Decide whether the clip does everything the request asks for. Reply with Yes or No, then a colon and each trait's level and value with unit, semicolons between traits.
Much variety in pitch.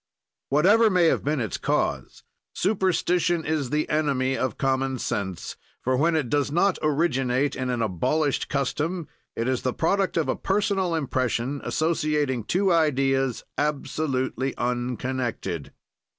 No: average, 4.2 semitones